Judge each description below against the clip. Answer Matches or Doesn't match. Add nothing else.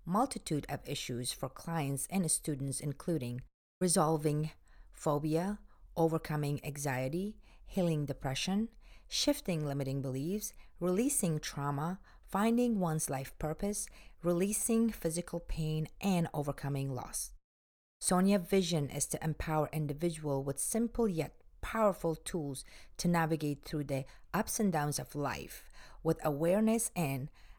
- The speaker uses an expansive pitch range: Doesn't match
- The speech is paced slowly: Matches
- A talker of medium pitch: Matches